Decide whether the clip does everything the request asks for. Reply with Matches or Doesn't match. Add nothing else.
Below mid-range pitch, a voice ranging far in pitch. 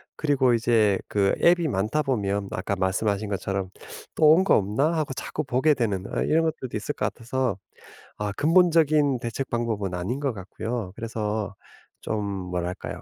Matches